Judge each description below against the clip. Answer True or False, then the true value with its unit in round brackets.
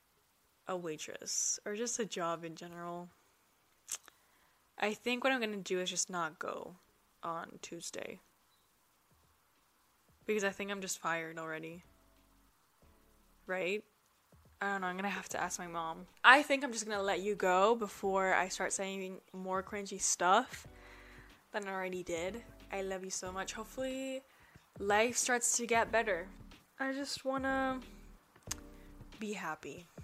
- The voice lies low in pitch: False (195 Hz)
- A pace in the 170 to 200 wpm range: False (145 wpm)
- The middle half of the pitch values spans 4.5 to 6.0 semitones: False (3.8 semitones)